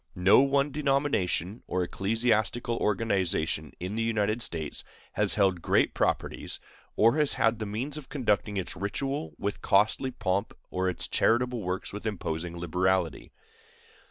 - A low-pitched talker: Yes, low, 105 Hz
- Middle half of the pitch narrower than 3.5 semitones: No, average, 4.7 semitones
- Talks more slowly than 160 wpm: Yes, average, 140 wpm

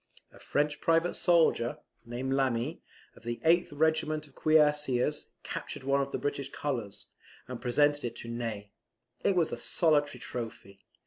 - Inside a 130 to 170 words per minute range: Yes, average, 150 wpm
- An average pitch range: Yes, average, 4.3 semitones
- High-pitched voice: No, medium, 140 Hz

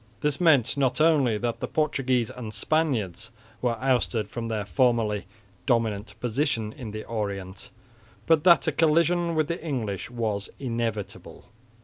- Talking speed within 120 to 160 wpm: Yes, average, 140 wpm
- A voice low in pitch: Yes, low, 120 Hz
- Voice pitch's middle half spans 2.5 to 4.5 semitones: No, wide, 5.5 semitones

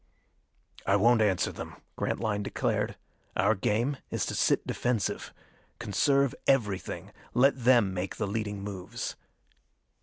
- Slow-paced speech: Yes, slow, 120 wpm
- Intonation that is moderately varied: Yes, average, 3.5 semitones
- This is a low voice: Yes, low, 110 Hz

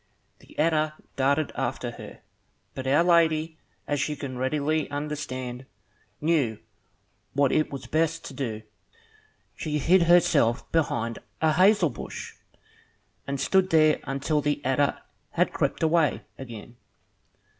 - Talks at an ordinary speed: No, slow, 125 wpm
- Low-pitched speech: No, medium, 150 Hz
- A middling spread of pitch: Yes, average, 3.2 semitones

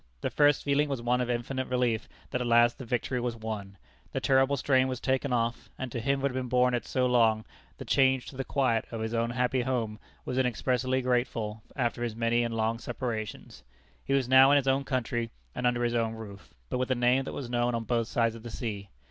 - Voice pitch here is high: No, low, 125 Hz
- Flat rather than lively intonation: Yes, narrow, 2.1 semitones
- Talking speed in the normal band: No, fast, 230 wpm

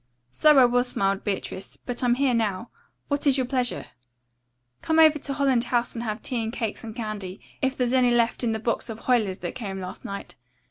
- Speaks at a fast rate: Yes, fast, 215 wpm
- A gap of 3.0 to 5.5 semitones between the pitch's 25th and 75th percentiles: Yes, average, 3.3 semitones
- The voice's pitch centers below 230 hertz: No, high, 240 Hz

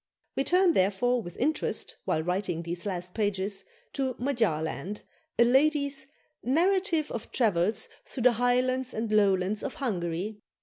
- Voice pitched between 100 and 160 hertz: No, high, 225 Hz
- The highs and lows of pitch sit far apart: Yes, wide, 6.0 semitones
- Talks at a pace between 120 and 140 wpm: Yes, slow, 135 wpm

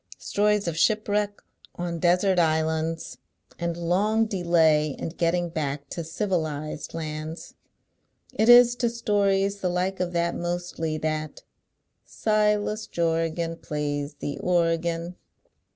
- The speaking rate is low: Yes, slow, 115 wpm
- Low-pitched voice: No, medium, 170 Hz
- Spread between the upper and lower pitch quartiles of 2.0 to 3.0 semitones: No, average, 3.8 semitones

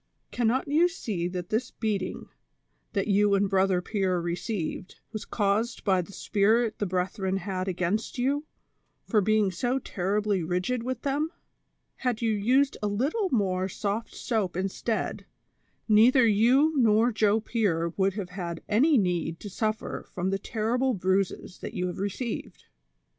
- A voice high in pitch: Yes, high, 205 Hz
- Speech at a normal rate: Yes, average, 150 wpm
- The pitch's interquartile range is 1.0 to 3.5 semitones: No, average, 3.9 semitones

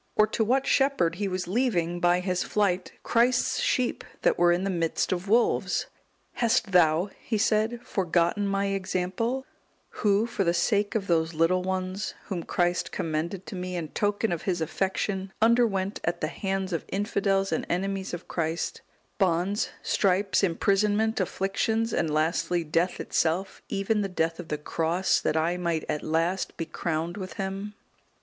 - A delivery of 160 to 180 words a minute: Yes, average, 165 wpm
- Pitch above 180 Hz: Yes, high, 190 Hz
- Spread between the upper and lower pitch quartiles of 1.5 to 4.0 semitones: Yes, average, 3.1 semitones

